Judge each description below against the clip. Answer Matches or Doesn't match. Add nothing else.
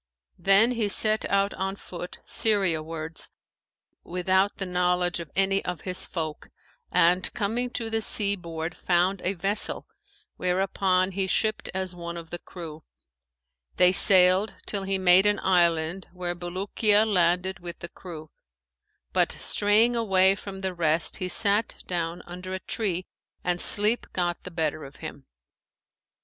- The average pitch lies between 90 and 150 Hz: Doesn't match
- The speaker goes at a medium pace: Matches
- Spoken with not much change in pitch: Matches